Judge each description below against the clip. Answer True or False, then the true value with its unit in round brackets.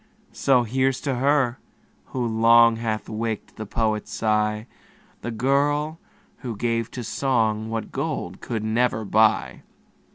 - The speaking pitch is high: False (115 Hz)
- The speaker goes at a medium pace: False (130 wpm)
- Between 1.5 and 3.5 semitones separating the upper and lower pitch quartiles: True (2.9 semitones)